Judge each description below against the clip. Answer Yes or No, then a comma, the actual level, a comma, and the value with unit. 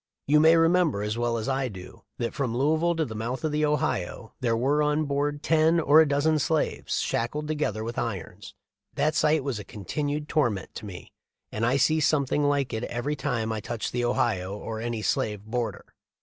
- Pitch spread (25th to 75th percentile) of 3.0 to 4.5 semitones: No, average, 5.0 semitones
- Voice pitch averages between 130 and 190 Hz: Yes, low, 135 Hz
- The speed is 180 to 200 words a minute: Yes, average, 195 wpm